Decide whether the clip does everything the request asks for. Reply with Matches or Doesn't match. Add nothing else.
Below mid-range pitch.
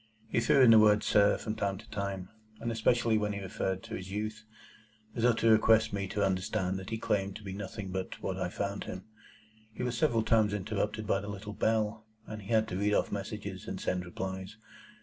Matches